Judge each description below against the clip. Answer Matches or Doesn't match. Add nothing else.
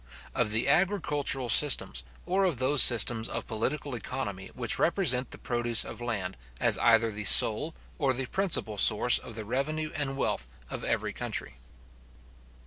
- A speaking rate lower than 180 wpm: Matches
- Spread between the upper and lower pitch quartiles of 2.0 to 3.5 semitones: Doesn't match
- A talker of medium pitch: Doesn't match